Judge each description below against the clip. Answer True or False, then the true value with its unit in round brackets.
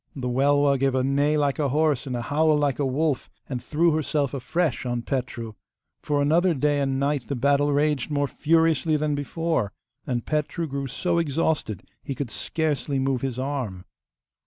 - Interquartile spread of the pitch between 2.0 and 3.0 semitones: True (2.4 semitones)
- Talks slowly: False (180 wpm)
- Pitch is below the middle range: False (145 Hz)